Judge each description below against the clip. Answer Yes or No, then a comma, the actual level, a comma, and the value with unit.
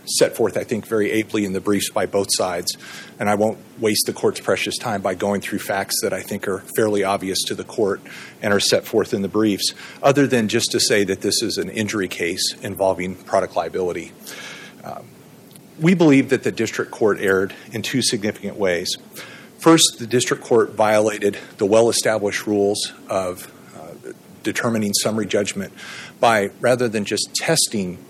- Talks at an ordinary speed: Yes, average, 180 wpm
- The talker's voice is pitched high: No, low, 105 Hz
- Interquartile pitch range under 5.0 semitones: Yes, average, 3.5 semitones